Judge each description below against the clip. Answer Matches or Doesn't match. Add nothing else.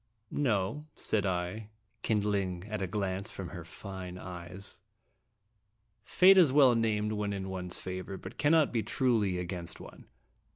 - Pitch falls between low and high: Doesn't match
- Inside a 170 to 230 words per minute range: Doesn't match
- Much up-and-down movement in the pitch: Doesn't match